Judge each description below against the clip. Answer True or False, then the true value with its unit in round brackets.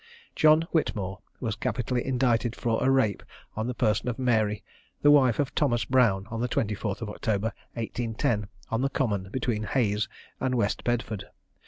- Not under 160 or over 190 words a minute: True (165 wpm)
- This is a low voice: True (115 Hz)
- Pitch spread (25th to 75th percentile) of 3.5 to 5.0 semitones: False (3.1 semitones)